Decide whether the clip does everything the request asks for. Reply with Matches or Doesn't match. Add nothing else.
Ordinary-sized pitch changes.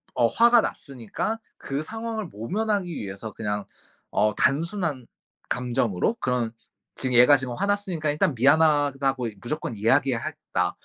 Doesn't match